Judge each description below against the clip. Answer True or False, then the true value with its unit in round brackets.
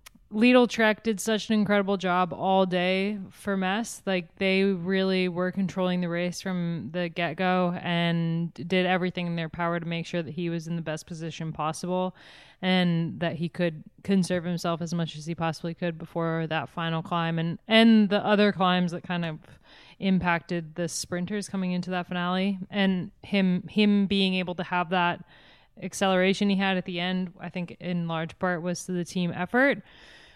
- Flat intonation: True (2.0 semitones)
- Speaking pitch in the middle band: True (180 Hz)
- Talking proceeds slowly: False (185 wpm)